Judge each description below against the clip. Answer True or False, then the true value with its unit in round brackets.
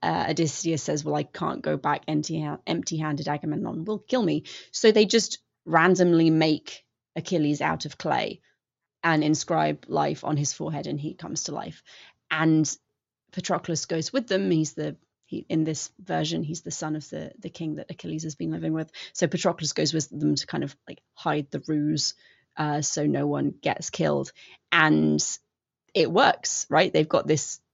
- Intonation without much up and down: True (2.1 semitones)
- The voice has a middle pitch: True (155 Hz)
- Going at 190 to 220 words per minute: False (180 wpm)